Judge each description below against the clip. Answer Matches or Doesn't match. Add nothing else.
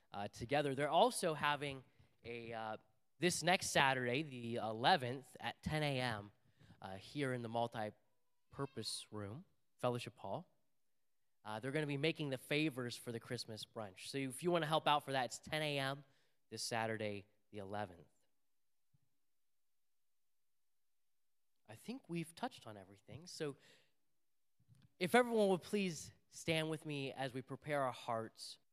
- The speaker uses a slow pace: Doesn't match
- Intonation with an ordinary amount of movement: Matches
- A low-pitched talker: Matches